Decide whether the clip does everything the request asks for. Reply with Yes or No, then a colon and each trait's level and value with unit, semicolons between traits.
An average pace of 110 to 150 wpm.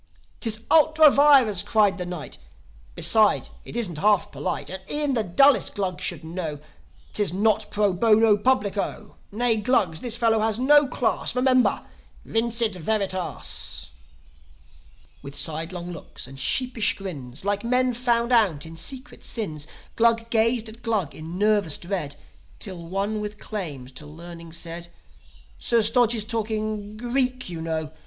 Yes: average, 145 wpm